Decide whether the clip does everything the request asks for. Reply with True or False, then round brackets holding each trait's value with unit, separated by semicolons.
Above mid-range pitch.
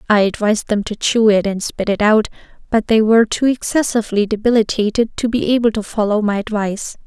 True (215 Hz)